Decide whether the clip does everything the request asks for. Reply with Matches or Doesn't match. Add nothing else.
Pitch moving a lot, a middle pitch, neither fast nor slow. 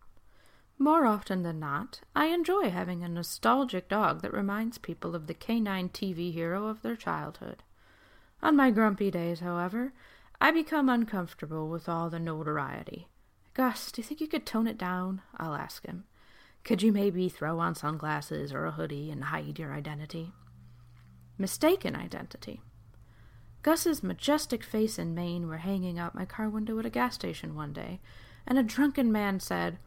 Matches